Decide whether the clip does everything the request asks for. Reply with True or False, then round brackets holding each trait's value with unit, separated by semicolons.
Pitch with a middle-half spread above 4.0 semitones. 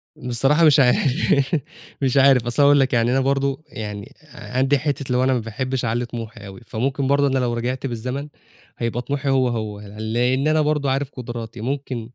False (2.8 semitones)